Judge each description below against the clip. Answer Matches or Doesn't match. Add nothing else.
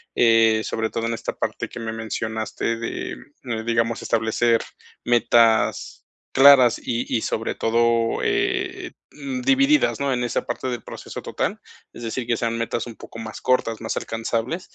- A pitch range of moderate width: Doesn't match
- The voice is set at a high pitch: Doesn't match